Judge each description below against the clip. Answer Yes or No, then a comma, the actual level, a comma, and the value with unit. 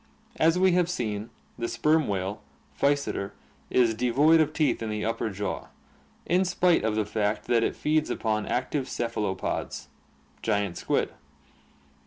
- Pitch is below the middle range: Yes, low, 115 Hz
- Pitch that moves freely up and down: Yes, wide, 6.4 semitones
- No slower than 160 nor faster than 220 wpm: No, average, 145 wpm